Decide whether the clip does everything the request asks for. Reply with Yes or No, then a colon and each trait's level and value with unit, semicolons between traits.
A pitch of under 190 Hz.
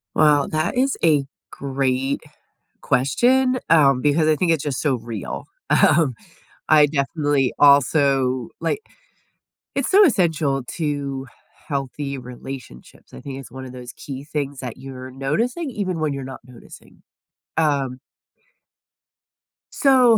Yes: medium, 140 Hz